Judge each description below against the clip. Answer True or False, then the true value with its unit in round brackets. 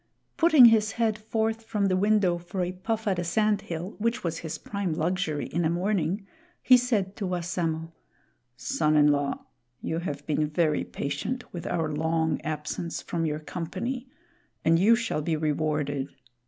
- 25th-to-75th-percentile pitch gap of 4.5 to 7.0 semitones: True (5.2 semitones)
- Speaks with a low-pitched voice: False (175 Hz)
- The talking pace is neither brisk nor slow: True (170 wpm)